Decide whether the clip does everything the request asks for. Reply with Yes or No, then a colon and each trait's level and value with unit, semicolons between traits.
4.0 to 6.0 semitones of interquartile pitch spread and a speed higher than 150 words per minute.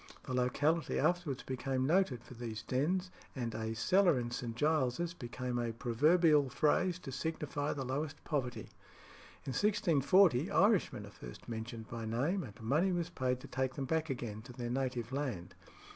Yes: average, 5.1 semitones; average, 165 wpm